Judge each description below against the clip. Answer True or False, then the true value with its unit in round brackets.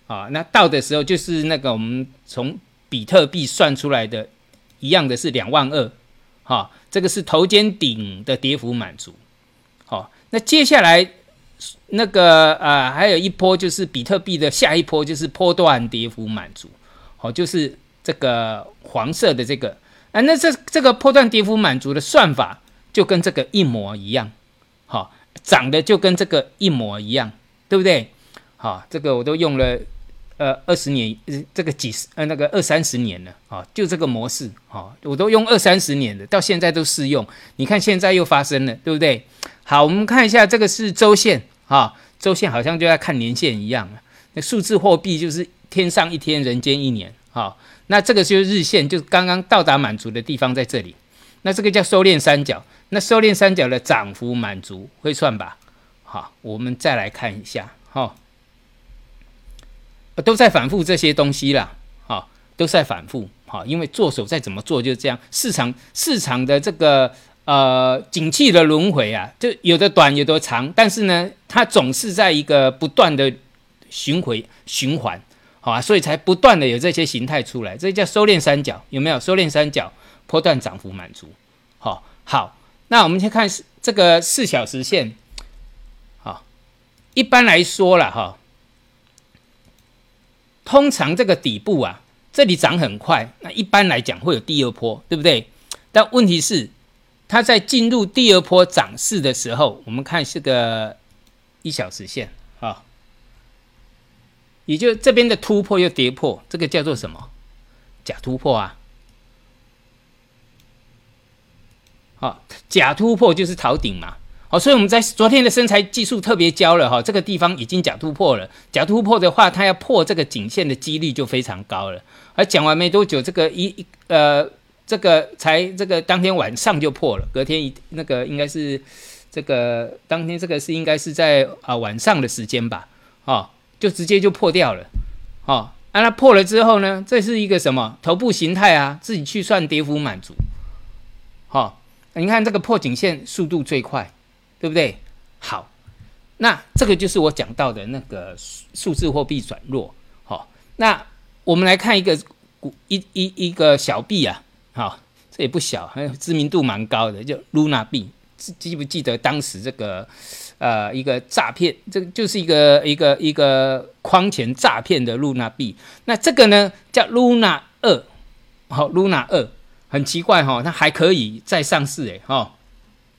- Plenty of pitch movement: True (7.1 semitones)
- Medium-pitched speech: True (155 Hz)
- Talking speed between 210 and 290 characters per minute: True (255 characters per minute)